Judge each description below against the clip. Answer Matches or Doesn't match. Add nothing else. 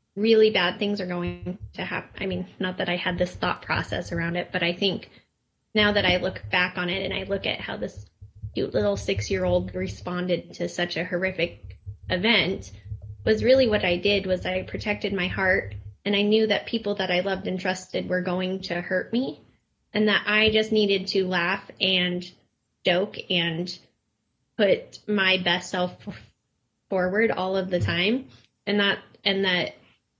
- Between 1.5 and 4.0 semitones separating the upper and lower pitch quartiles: Matches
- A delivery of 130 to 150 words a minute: Doesn't match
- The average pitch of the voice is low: Doesn't match